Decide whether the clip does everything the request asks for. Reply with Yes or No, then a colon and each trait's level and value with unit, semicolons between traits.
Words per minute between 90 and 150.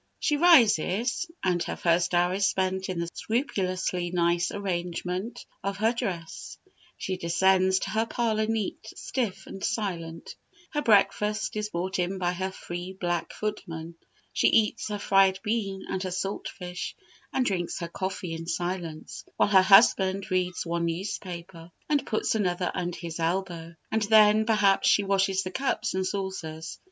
No: average, 160 wpm